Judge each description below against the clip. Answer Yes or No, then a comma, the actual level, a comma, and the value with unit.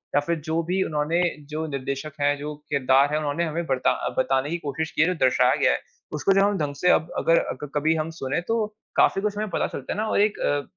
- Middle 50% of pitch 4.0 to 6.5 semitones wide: No, average, 3.2 semitones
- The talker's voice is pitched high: No, medium, 155 Hz